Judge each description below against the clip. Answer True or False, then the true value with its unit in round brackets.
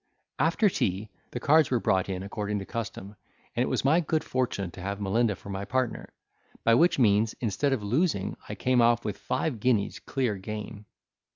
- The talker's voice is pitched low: True (110 Hz)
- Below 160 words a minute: False (190 wpm)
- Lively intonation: False (4.4 semitones)